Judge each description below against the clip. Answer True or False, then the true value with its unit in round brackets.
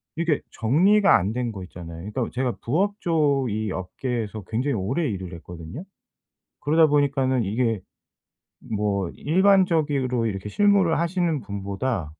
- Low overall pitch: True (125 Hz)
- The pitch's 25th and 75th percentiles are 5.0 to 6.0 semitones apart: False (7.8 semitones)